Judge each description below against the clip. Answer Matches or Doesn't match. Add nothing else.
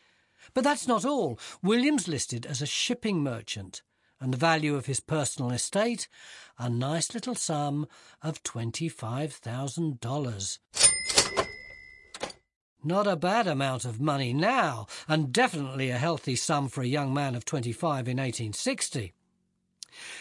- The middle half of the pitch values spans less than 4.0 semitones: Doesn't match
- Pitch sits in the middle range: Matches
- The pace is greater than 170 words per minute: Doesn't match